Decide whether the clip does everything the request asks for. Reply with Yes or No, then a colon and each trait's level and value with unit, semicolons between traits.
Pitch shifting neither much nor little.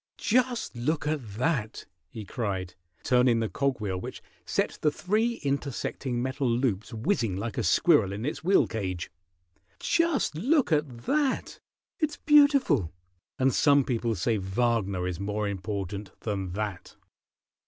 No: wide, 6.9 semitones